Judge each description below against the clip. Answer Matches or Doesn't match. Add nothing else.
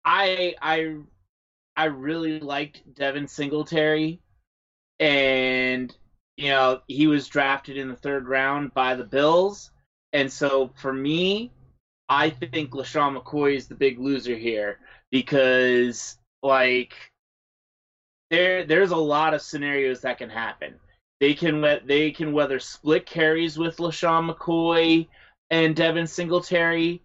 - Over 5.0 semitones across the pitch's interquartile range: Doesn't match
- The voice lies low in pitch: Doesn't match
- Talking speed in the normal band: Doesn't match